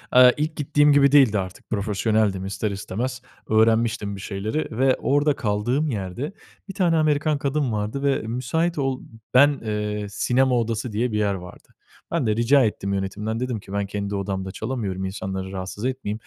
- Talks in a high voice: No, low, 110 Hz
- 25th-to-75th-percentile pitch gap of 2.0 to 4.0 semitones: No, average, 4.9 semitones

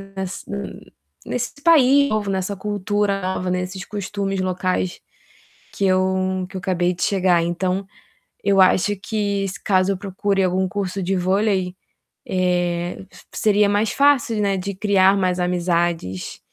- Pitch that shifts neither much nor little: No, narrow, 1.8 semitones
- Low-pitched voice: No, high, 190 Hz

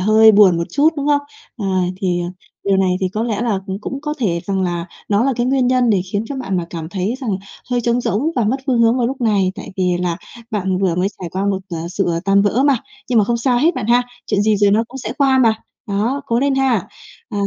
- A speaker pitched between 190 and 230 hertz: Yes, high, 215 Hz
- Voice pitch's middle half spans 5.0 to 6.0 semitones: No, average, 4.6 semitones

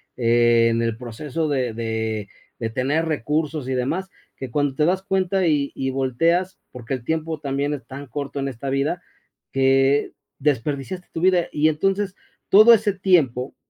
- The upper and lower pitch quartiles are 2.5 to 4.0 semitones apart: No, average, 4.5 semitones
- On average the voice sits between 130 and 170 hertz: Yes, medium, 140 Hz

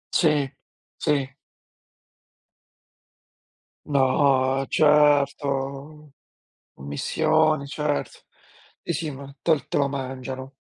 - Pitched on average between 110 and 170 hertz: Yes, medium, 140 Hz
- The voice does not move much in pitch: Yes, narrow, 2.0 semitones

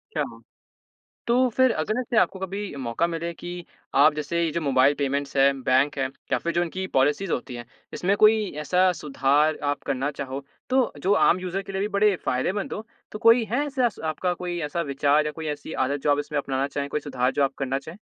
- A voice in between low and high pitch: Yes, medium, 155 Hz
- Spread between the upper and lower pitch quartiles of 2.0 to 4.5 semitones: No, wide, 5.5 semitones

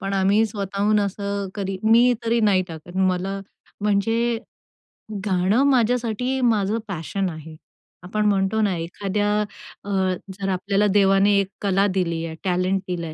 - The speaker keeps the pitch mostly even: Yes, narrow, 2.0 semitones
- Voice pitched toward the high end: Yes, high, 195 Hz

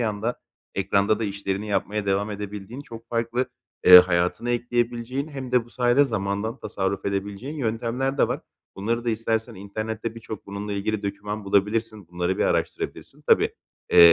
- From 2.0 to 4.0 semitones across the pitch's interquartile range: Yes, average, 2.9 semitones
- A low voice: Yes, low, 110 Hz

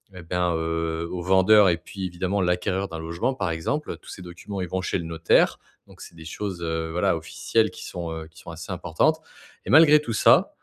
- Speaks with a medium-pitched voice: No, very low, 90 Hz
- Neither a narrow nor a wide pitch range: Yes, average, 3.0 semitones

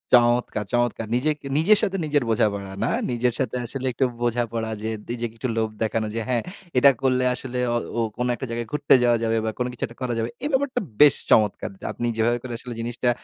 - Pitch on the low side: Yes, low, 120 Hz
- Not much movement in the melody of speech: Yes, narrow, 2.3 semitones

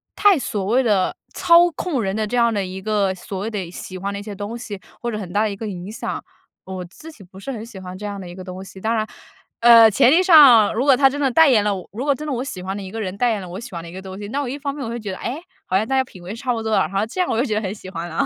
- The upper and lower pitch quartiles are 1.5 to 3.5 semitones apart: No, average, 4.5 semitones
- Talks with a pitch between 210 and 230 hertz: Yes, high, 215 Hz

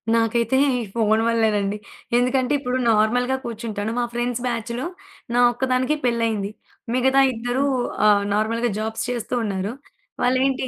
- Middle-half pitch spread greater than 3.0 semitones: No, narrow, 2.4 semitones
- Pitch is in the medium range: No, high, 235 Hz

